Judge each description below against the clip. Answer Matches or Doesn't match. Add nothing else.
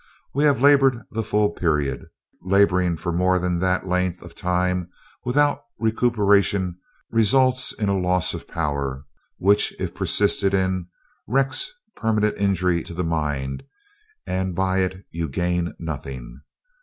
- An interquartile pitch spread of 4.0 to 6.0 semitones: Doesn't match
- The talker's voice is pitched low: Matches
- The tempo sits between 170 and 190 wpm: Doesn't match